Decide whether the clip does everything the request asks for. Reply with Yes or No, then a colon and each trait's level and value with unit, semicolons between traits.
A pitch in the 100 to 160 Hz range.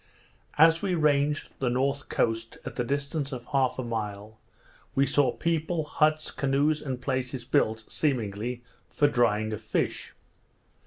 Yes: low, 135 Hz